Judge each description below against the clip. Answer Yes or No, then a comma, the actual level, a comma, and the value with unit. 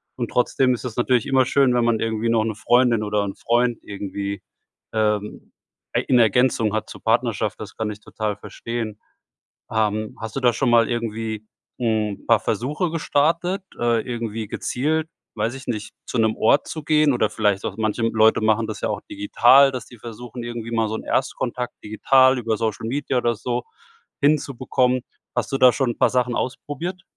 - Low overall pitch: Yes, low, 120 Hz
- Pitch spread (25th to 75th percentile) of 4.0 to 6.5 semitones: No, average, 2.8 semitones